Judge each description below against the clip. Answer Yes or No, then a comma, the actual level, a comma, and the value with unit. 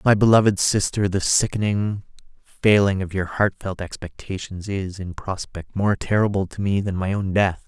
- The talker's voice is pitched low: Yes, low, 100 Hz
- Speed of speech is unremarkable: Yes, average, 170 wpm